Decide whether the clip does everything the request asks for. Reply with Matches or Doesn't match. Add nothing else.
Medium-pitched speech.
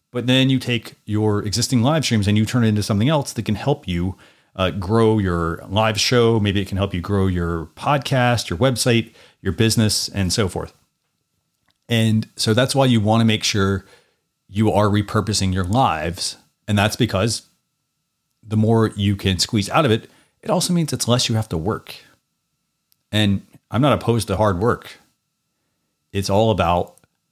Doesn't match